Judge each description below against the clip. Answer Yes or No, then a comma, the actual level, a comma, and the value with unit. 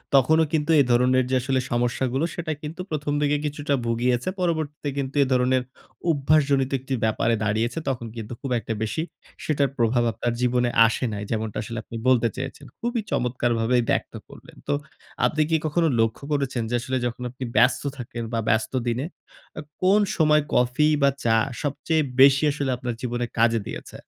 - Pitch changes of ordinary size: Yes, average, 3.6 semitones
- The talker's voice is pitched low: Yes, low, 130 Hz